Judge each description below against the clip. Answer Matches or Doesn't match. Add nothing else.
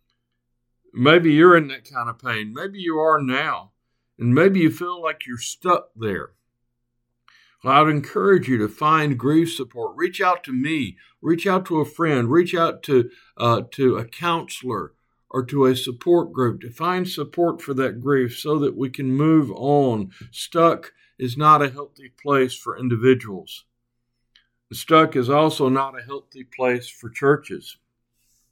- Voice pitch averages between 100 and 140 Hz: Matches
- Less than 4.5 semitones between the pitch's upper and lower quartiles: Doesn't match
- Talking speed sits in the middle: Matches